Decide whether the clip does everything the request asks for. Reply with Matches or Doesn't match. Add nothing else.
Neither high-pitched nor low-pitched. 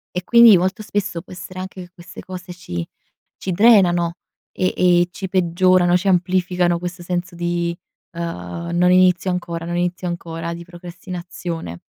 Matches